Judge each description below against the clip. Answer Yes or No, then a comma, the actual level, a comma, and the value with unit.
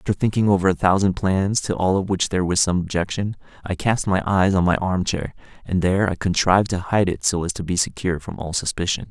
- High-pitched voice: No, very low, 95 Hz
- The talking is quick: Yes, fast, 245 wpm